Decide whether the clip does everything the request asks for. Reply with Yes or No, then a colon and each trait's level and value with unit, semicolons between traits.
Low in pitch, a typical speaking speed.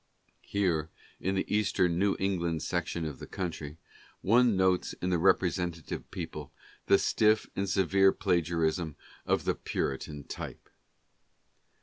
No: very low, 90 Hz; slow, 125 wpm